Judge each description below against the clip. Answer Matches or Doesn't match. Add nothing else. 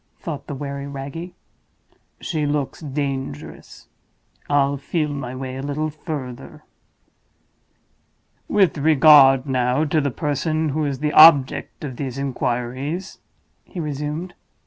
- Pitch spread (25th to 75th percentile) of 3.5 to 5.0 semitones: Doesn't match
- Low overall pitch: Doesn't match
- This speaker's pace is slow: Matches